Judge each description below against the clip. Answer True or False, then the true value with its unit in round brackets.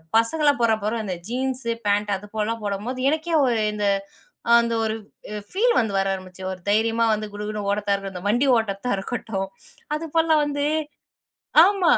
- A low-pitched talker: False (225 Hz)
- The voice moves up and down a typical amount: True (4.3 semitones)